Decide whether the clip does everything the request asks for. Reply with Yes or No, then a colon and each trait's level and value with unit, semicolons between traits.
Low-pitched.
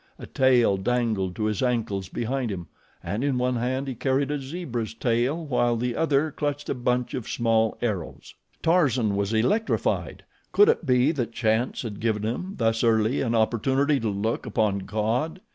Yes: low, 120 Hz